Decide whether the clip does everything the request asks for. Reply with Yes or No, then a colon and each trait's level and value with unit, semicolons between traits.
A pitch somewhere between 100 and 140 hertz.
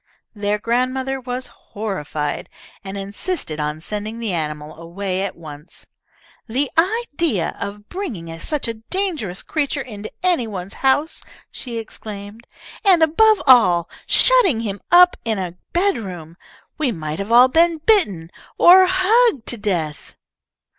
No: high, 225 Hz